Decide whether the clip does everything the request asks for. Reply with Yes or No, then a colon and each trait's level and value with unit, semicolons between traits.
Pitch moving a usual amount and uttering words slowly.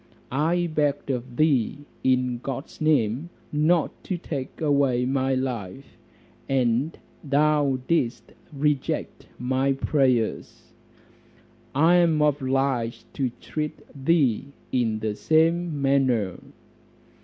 Yes: average, 3.3 semitones; slow, 100 wpm